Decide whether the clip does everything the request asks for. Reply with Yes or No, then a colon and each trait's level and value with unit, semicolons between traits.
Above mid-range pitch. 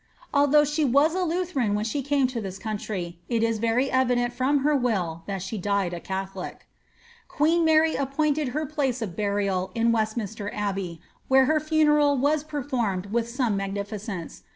Yes: high, 240 Hz